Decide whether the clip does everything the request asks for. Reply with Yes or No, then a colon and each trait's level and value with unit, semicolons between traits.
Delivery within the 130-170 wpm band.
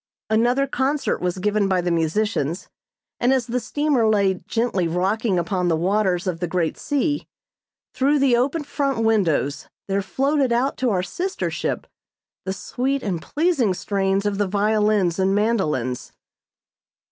Yes: average, 150 wpm